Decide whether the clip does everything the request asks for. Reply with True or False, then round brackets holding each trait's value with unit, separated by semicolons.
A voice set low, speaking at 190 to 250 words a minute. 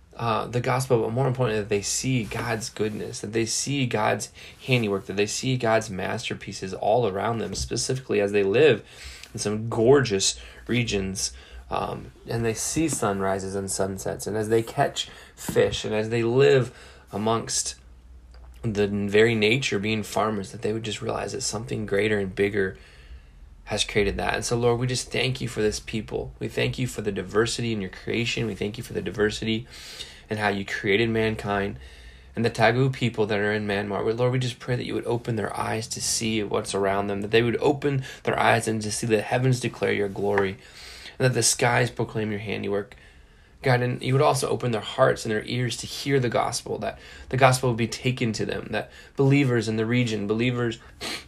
True (110 Hz; 200 wpm)